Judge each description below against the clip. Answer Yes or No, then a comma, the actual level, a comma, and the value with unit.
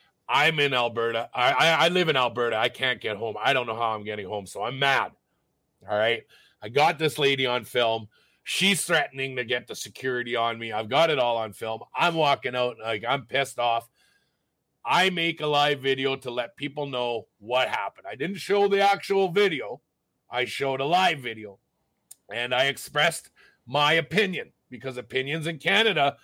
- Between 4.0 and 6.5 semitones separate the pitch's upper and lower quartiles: Yes, wide, 5.5 semitones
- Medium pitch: No, low, 130 Hz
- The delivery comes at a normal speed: Yes, average, 190 wpm